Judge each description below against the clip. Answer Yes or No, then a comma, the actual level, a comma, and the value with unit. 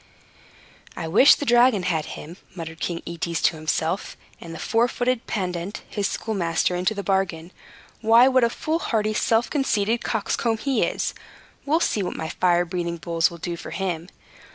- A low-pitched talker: No, high, 190 Hz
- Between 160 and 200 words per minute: Yes, average, 170 wpm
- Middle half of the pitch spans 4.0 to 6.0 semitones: Yes, average, 5.1 semitones